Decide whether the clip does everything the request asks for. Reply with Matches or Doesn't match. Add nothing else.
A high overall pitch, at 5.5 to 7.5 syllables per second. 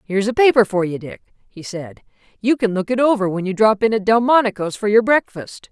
Matches